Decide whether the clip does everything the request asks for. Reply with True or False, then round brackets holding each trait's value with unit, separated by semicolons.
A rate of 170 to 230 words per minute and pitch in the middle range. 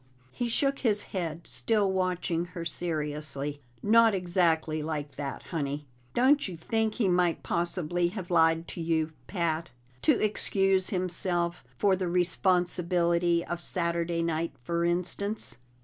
False (135 wpm; 175 Hz)